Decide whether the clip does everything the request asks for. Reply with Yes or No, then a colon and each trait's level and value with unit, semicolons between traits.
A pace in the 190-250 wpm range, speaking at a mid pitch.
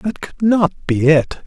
Yes: fast, 205 wpm; medium, 175 Hz